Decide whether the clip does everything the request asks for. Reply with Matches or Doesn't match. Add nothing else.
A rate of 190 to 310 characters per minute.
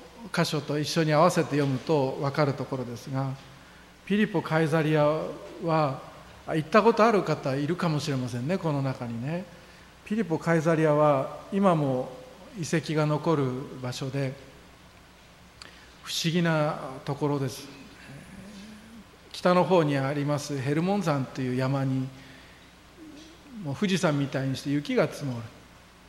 Matches